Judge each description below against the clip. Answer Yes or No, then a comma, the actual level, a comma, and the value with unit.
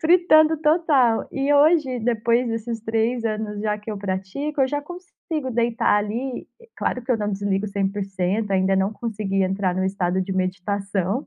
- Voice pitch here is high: Yes, high, 220 Hz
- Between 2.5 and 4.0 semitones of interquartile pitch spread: No, average, 5.0 semitones